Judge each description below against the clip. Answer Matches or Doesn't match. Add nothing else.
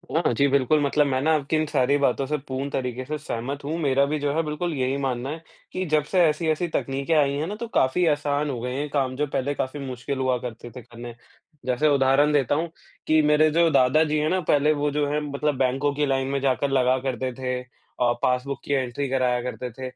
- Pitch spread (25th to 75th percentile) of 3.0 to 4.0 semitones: Doesn't match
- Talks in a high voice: Doesn't match